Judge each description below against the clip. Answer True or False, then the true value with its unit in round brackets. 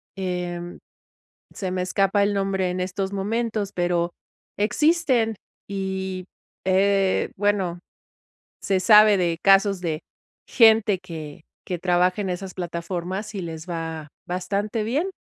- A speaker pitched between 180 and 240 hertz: True (190 Hz)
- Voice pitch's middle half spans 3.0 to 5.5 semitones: False (2.5 semitones)